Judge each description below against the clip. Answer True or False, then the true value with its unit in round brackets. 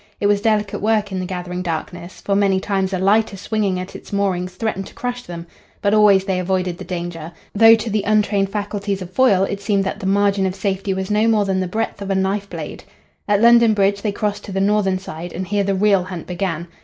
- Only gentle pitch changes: True (1.9 semitones)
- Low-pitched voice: False (195 Hz)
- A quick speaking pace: True (235 wpm)